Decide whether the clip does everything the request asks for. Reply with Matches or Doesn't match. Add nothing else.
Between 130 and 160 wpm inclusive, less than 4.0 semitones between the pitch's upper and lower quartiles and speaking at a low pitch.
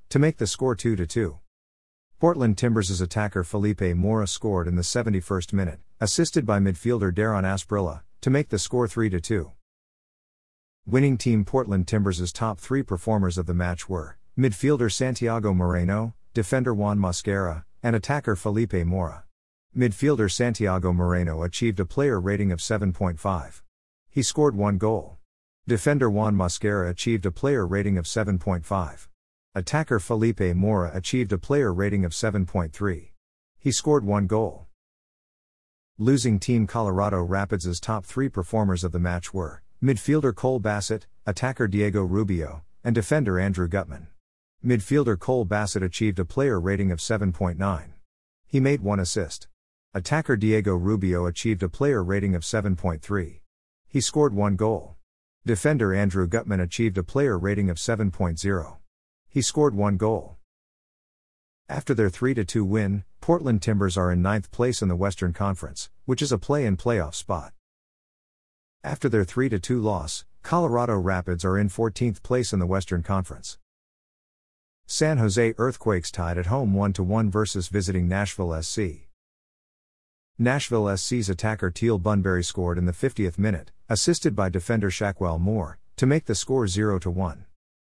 Doesn't match